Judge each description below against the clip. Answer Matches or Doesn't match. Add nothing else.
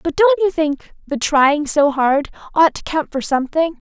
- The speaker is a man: Doesn't match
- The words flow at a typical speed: Matches